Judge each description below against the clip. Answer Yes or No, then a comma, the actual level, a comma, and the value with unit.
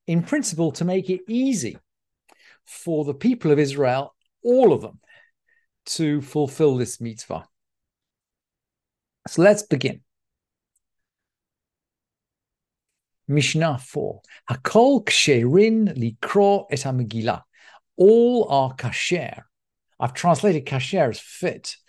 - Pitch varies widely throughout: Yes, wide, 7.5 semitones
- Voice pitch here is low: No, medium, 160 Hz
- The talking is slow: Yes, slow, 90 wpm